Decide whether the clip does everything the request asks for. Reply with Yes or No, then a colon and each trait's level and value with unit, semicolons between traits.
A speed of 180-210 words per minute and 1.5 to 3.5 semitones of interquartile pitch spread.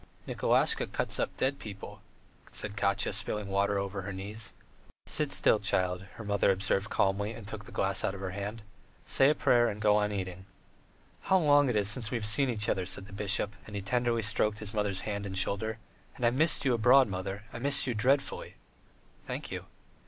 Yes: fast, 205 wpm; average, 2.9 semitones